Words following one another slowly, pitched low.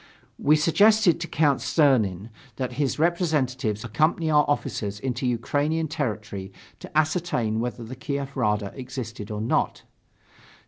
Yes: slow, 130 wpm; low, 130 Hz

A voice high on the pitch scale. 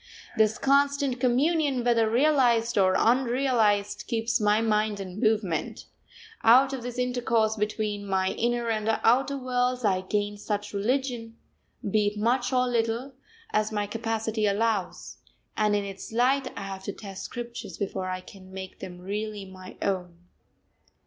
Yes: high, 220 Hz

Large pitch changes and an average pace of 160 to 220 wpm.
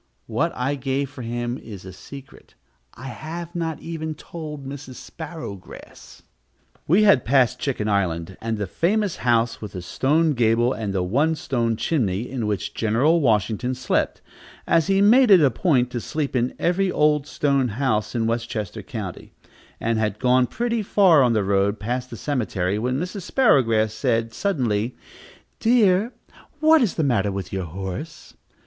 Yes: wide, 6.4 semitones; average, 165 wpm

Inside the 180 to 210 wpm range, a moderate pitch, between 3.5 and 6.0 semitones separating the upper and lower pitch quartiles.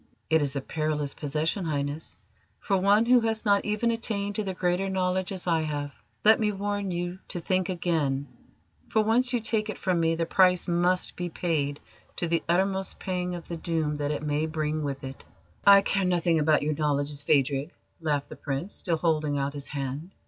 Yes: average, 200 wpm; medium, 170 Hz; average, 4.4 semitones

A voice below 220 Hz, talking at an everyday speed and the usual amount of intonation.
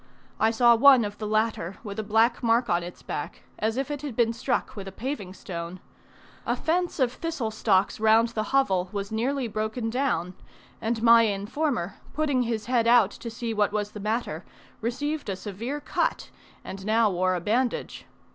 No: high, 225 Hz; average, 185 wpm; average, 3.2 semitones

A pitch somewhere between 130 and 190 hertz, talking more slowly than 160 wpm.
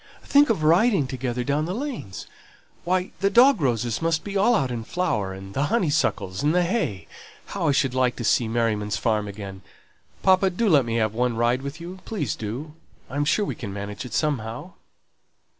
No: low, 135 Hz; average, 190 wpm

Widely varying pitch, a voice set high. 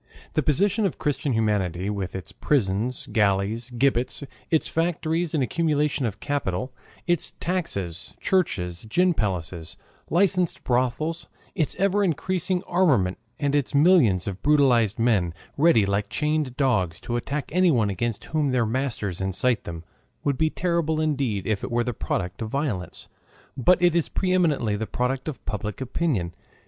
No: wide, 7.4 semitones; low, 130 Hz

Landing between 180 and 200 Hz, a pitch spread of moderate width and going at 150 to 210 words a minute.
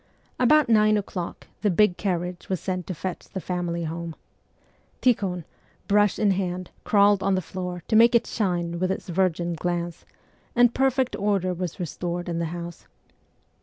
Yes: medium, 185 Hz; average, 3.0 semitones; average, 165 wpm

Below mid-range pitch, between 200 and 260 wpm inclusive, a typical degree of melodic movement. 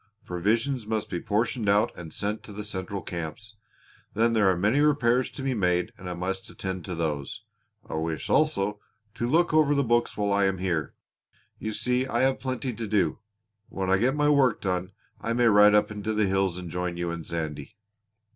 Yes: low, 105 Hz; fast, 205 wpm; average, 4.6 semitones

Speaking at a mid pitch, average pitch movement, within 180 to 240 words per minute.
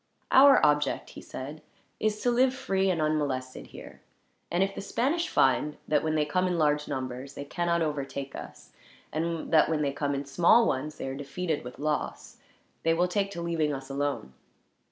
Yes: medium, 155 Hz; average, 4.2 semitones; average, 190 wpm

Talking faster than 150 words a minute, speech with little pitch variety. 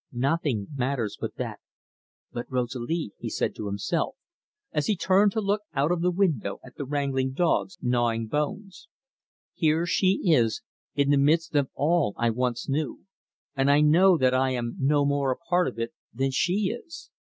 No: average, 175 wpm; average, 5.3 semitones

